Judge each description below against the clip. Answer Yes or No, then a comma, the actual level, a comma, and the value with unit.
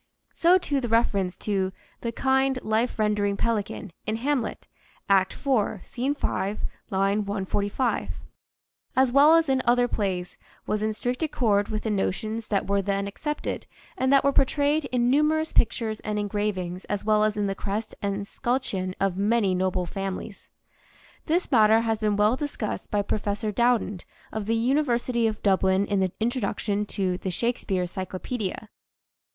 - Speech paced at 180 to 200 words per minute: No, average, 160 wpm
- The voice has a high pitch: Yes, high, 215 Hz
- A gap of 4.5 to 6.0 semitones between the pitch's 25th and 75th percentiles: No, average, 3.7 semitones